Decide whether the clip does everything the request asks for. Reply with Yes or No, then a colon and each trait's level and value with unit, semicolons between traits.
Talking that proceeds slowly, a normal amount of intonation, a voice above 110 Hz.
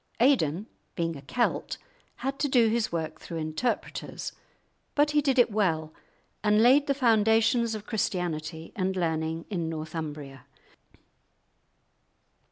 No: slow, 125 wpm; wide, 6.8 semitones; high, 190 Hz